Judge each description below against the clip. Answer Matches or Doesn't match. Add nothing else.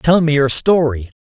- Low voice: Doesn't match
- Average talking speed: Matches